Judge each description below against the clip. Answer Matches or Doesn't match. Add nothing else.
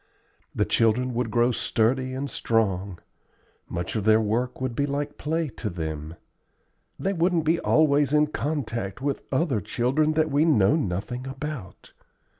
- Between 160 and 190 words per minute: Doesn't match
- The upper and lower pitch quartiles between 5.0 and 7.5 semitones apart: Matches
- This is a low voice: Matches